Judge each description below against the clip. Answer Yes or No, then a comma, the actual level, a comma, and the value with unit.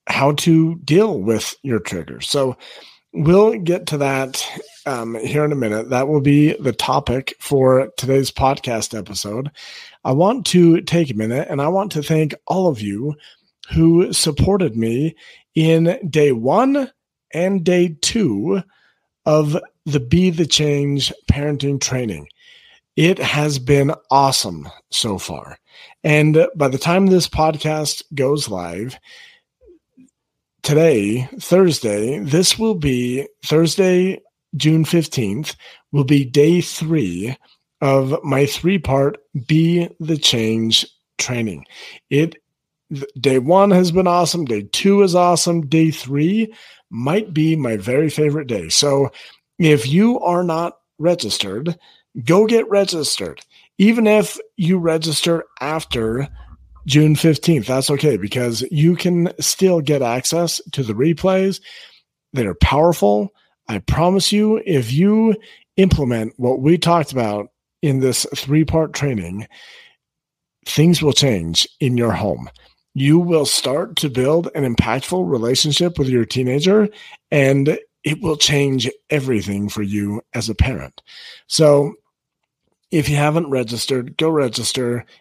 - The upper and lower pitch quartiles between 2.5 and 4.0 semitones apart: No, average, 4.8 semitones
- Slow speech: Yes, slow, 130 wpm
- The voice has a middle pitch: Yes, medium, 150 Hz